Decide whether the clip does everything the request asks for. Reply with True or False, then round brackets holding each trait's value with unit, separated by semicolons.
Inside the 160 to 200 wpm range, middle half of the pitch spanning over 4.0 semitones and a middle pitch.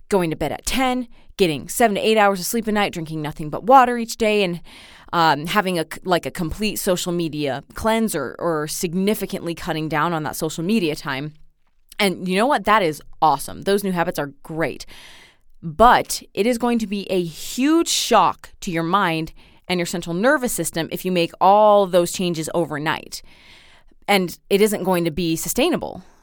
True (190 wpm; 4.4 semitones; 180 Hz)